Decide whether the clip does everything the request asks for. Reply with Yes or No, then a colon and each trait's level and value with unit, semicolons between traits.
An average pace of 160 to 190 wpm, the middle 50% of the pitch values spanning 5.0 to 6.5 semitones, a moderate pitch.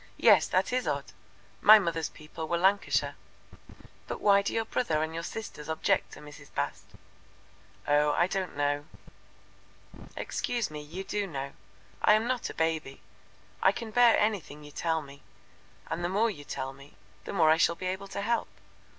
Yes: average, 175 wpm; average, 5.3 semitones; medium, 170 Hz